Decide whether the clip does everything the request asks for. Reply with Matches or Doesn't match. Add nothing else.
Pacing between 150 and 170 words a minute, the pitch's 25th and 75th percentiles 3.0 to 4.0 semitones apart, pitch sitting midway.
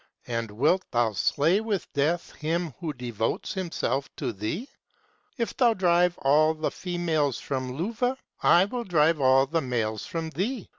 Doesn't match